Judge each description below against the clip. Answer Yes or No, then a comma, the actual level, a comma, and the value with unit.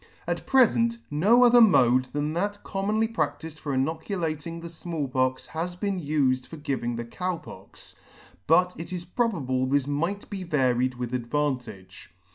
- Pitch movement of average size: No, wide, 6.0 semitones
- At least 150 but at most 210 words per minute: Yes, average, 155 wpm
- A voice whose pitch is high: No, medium, 160 Hz